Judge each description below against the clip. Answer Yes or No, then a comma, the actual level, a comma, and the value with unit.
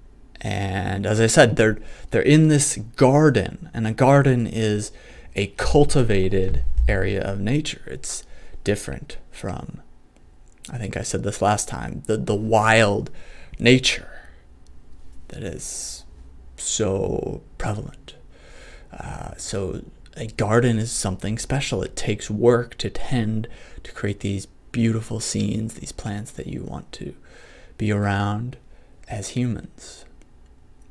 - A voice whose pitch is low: Yes, low, 105 Hz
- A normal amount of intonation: Yes, average, 3.6 semitones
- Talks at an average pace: No, slow, 120 wpm